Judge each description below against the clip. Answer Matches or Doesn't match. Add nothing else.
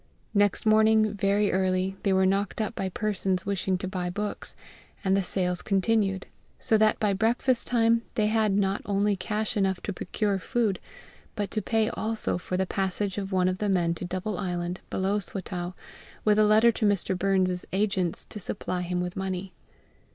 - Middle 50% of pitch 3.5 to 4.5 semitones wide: Doesn't match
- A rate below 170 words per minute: Doesn't match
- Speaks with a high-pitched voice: Matches